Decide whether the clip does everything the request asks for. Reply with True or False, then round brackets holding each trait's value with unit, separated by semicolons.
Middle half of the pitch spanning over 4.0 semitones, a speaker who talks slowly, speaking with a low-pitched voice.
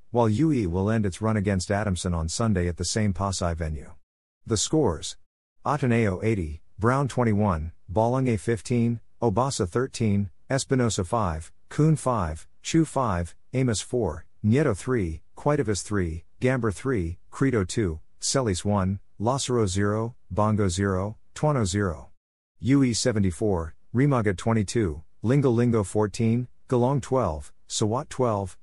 True (5.0 semitones; 125 wpm; 105 Hz)